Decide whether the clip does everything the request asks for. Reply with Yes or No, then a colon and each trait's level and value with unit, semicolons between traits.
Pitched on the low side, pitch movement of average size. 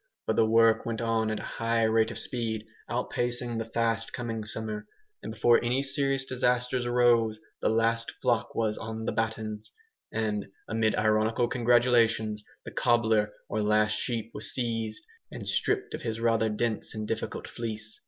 No: low, 115 Hz; narrow, 1.4 semitones